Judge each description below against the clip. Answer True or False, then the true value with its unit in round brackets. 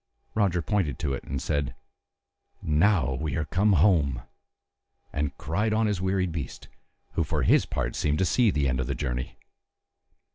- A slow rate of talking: False (170 wpm)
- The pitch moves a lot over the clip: True (5.7 semitones)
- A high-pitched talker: False (80 Hz)